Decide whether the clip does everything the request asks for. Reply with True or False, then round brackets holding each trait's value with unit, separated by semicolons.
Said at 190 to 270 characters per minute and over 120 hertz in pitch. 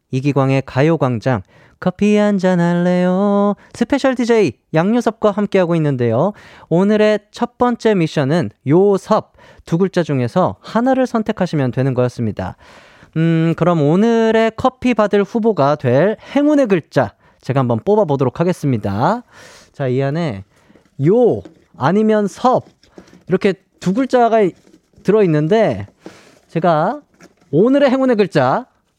True (265 characters per minute; 185 Hz)